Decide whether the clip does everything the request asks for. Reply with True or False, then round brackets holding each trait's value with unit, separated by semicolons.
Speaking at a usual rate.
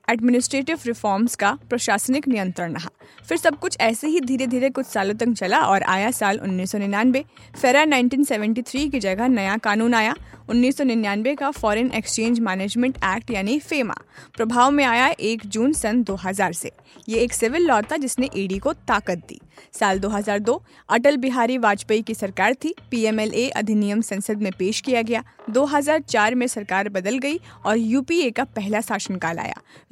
True (140 wpm)